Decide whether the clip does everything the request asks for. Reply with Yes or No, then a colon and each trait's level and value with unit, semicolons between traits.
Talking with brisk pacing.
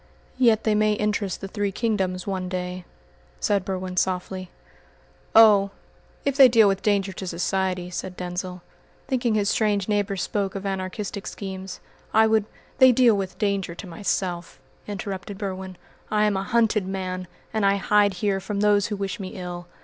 No: average, 170 wpm